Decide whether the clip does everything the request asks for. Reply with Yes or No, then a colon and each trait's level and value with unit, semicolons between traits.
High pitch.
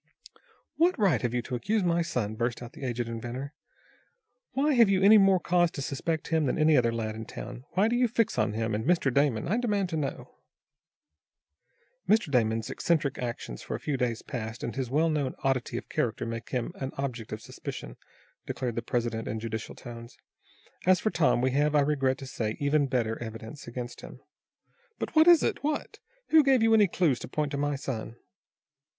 No: low, 135 Hz